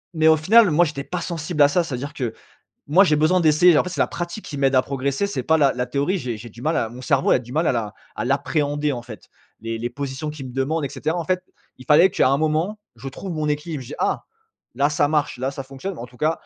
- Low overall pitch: No, medium, 145 Hz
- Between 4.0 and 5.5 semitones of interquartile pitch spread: No, average, 3.5 semitones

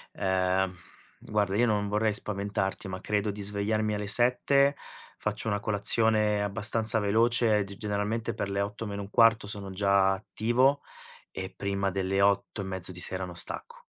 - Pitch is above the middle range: No, low, 105 Hz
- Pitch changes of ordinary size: No, narrow, 1.9 semitones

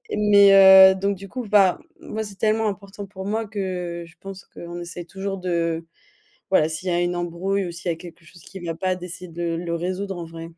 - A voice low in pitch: No, medium, 180 Hz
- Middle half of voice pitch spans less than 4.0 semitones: Yes, narrow, 2.5 semitones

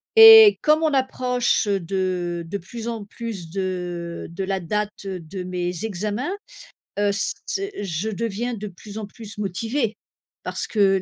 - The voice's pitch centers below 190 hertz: No, high, 205 Hz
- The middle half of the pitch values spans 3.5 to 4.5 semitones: Yes, average, 4.1 semitones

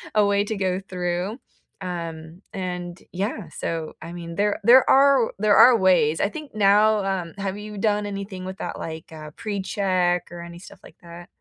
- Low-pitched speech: No, high, 190 Hz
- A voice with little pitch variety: No, average, 3.1 semitones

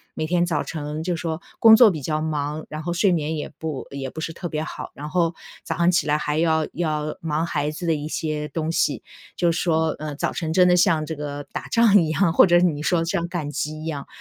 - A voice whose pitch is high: No, medium, 160 Hz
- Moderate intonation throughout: No, narrow, 2.2 semitones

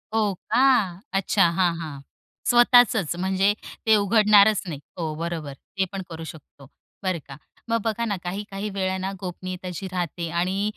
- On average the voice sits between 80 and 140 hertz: No, high, 190 Hz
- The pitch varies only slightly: No, average, 3.4 semitones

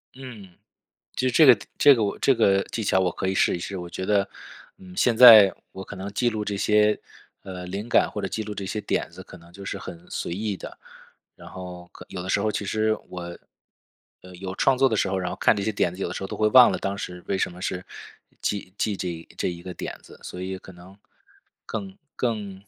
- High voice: No, low, 100 Hz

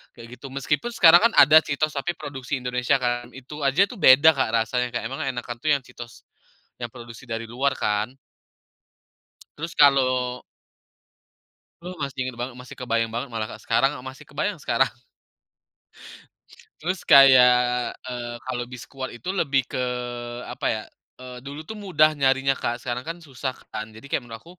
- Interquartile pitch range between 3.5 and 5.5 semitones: No, average, 2.8 semitones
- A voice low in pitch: Yes, low, 130 Hz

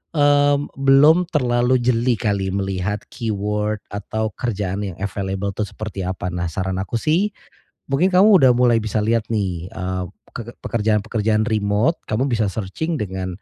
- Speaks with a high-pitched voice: No, low, 110 Hz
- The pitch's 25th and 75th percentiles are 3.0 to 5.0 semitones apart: Yes, average, 4.3 semitones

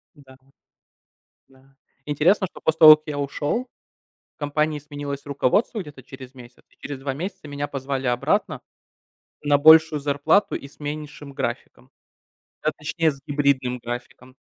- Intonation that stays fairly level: Yes, narrow, 2.1 semitones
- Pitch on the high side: No, medium, 145 Hz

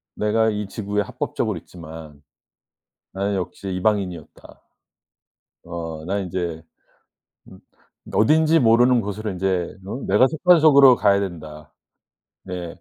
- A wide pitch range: No, average, 4.4 semitones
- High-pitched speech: No, low, 100 Hz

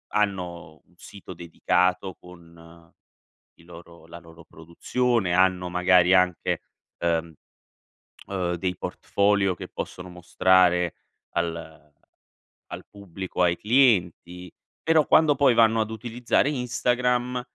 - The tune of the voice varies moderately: Yes, average, 4.3 semitones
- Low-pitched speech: Yes, very low, 90 Hz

